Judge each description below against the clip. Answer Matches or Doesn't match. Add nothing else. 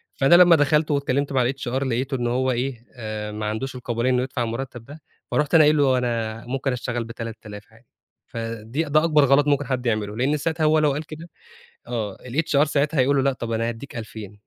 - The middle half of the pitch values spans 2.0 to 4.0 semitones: Matches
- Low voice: Matches